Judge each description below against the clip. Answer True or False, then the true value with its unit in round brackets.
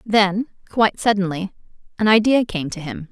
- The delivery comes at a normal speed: True (155 wpm)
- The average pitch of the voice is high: True (200 Hz)